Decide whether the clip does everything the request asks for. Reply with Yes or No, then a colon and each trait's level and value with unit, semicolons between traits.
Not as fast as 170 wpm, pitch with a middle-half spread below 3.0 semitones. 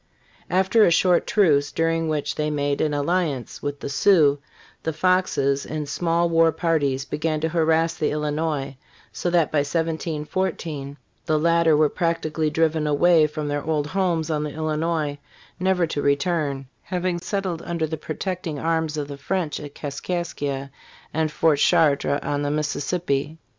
Yes: average, 155 wpm; narrow, 2.6 semitones